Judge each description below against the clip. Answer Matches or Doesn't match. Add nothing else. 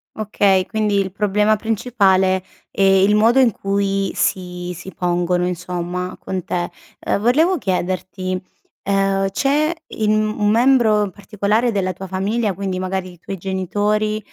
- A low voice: Doesn't match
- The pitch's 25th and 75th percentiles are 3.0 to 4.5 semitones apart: Doesn't match